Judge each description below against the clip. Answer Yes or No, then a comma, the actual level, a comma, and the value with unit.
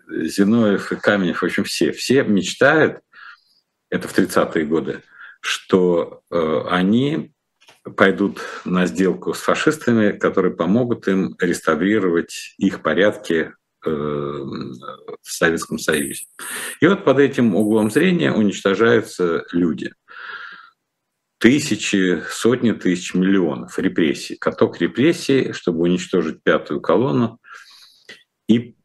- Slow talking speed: Yes, slow, 105 wpm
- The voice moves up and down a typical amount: Yes, average, 4.6 semitones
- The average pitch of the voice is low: Yes, low, 100 Hz